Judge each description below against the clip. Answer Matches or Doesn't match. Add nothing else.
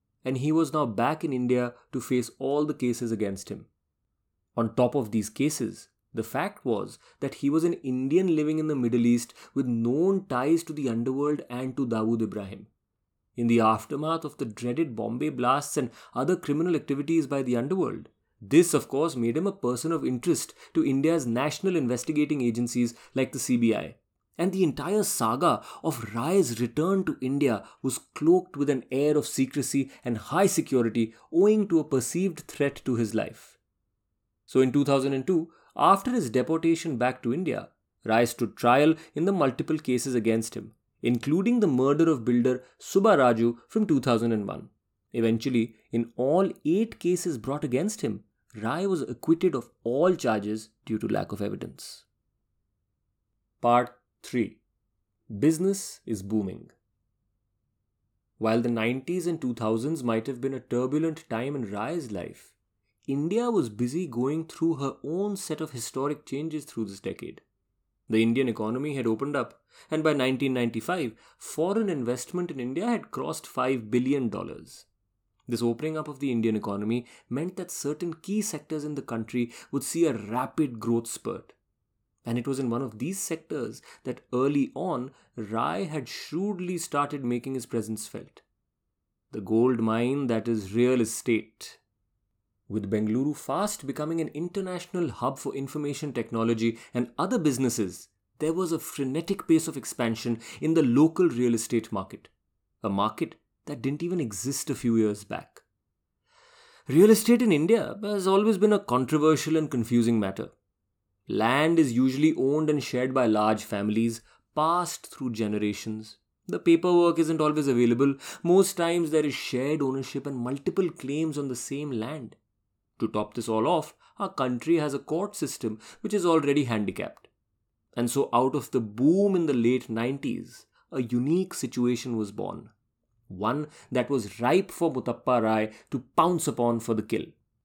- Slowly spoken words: Doesn't match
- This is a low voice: Matches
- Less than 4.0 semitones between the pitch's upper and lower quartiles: Doesn't match